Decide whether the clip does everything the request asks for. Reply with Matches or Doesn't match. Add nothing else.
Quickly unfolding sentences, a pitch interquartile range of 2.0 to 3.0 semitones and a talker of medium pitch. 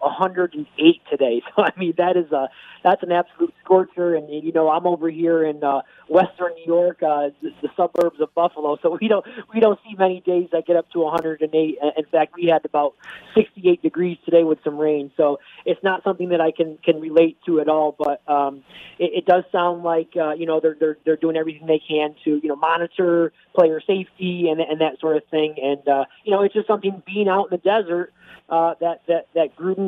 Matches